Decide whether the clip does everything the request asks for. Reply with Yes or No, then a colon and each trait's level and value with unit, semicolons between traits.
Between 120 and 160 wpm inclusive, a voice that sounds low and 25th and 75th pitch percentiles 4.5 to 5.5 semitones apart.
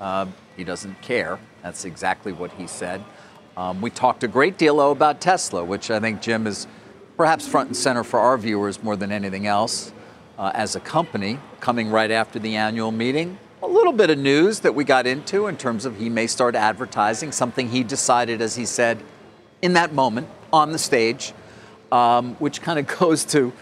No: average, 200 wpm; low, 120 Hz; average, 4.9 semitones